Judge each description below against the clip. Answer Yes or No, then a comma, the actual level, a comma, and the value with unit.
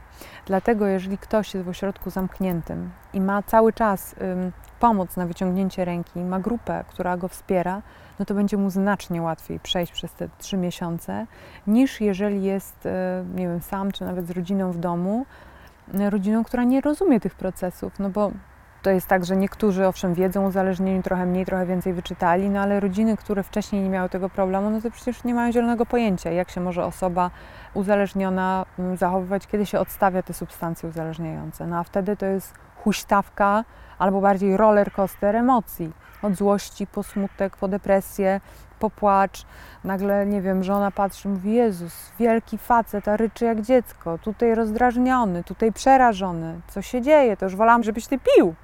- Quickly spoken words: Yes, fast, 175 wpm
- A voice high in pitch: Yes, high, 195 Hz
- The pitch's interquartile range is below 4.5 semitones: Yes, narrow, 2.4 semitones